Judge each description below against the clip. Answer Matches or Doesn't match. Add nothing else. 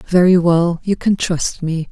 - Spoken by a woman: Matches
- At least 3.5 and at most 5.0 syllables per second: Matches